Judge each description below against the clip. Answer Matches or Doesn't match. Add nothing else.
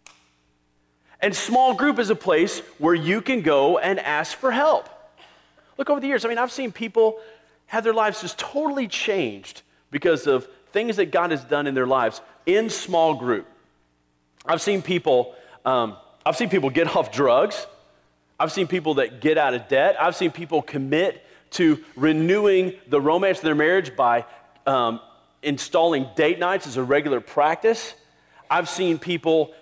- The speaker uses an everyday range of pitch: Doesn't match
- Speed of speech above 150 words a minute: Matches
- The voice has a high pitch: Doesn't match